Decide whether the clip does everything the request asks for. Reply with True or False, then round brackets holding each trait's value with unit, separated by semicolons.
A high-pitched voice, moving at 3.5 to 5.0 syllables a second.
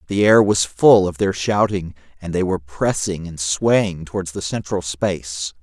False (90 Hz; 4.5 syllables/s)